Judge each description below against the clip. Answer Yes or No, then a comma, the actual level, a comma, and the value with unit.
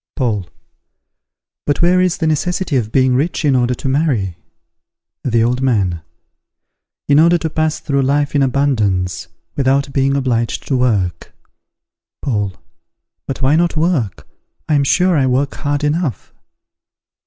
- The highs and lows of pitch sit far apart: No, average, 4.0 semitones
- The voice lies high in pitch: No, low, 135 Hz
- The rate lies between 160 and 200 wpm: No, average, 145 wpm